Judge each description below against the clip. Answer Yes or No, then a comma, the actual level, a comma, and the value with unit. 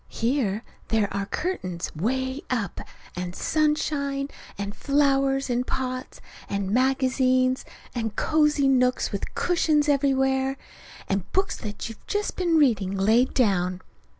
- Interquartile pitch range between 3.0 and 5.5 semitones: Yes, average, 5.1 semitones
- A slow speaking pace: Yes, slow, 125 wpm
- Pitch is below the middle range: No, very high, 255 Hz